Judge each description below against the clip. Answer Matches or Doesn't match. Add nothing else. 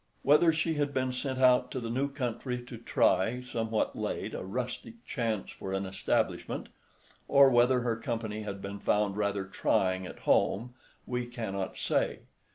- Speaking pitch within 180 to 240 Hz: Doesn't match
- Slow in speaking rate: Doesn't match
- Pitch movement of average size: Matches